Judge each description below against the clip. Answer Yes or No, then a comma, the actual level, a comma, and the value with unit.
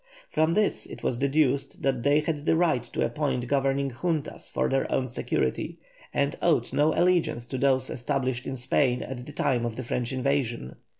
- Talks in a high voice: No, low, 135 Hz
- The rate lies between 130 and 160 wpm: No, average, 185 wpm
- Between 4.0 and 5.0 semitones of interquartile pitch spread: No, average, 2.9 semitones